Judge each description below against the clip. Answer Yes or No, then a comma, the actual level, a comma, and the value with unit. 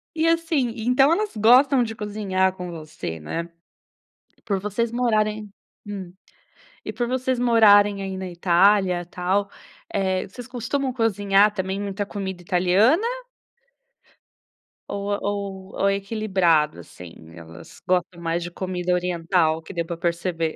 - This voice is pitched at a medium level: No, high, 195 Hz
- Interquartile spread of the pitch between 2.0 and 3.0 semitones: No, average, 3.7 semitones